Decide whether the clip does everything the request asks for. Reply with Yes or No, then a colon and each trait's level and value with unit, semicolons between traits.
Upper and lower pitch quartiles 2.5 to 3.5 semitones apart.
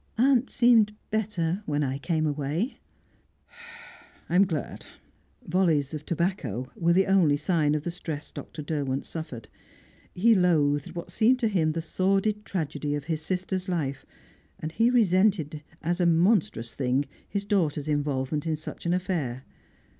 No: average, 4.5 semitones